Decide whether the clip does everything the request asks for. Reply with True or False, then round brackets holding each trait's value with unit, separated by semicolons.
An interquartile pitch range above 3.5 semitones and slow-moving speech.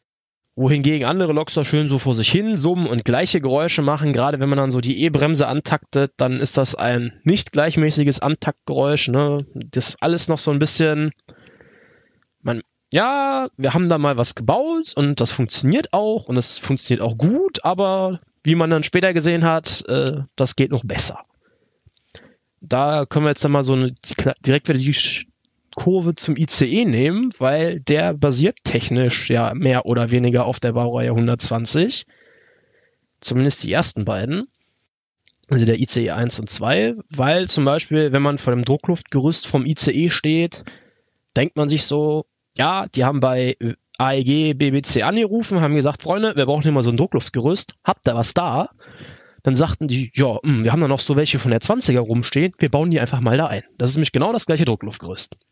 False (4.1 semitones; 180 wpm)